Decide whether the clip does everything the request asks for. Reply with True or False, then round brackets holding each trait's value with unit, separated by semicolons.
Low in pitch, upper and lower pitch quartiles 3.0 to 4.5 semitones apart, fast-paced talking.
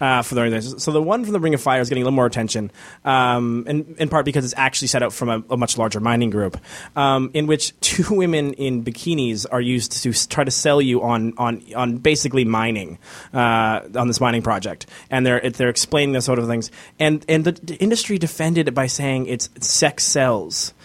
True (125 Hz; 3.9 semitones; 215 wpm)